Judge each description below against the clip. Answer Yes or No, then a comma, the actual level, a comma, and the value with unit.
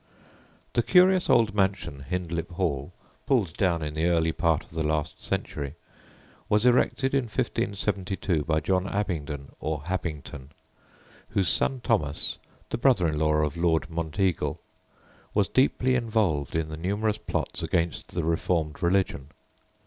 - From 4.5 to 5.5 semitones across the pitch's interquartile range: Yes, average, 4.9 semitones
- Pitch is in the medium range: No, very low, 85 Hz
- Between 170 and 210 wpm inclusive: No, average, 140 wpm